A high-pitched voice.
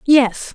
Yes: very high, 260 Hz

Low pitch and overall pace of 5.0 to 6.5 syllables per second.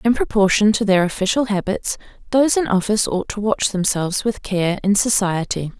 No: high, 205 Hz; 5.5 syllables/s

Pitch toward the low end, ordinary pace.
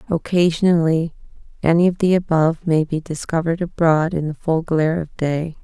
No: medium, 165 Hz; average, 160 wpm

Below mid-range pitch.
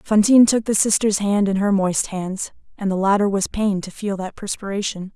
No: high, 200 Hz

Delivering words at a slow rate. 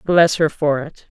No: average, 200 wpm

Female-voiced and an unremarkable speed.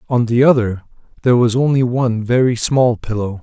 No: male; average, 175 wpm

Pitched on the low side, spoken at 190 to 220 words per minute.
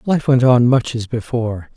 Yes: low, 120 Hz; fast, 205 wpm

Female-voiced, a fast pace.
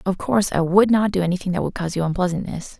Yes: female; fast, 255 wpm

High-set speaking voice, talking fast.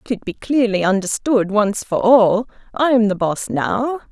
No: high, 220 Hz; average, 160 wpm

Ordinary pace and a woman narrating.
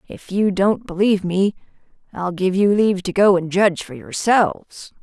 Yes: average, 180 wpm; female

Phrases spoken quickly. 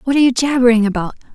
Yes: fast, 225 wpm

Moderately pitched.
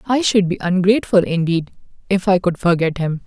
Yes: medium, 180 Hz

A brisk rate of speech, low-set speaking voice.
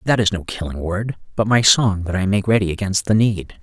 Yes: fast, 250 wpm; low, 100 Hz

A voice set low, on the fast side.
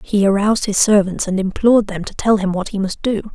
No: high, 200 Hz; fast, 250 wpm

